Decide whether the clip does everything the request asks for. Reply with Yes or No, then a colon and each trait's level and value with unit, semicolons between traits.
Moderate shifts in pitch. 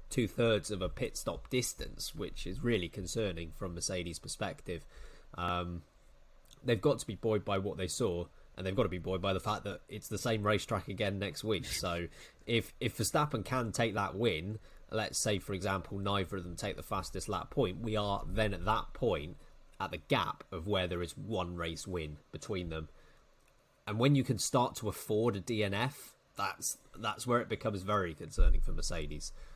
Yes: average, 4.0 semitones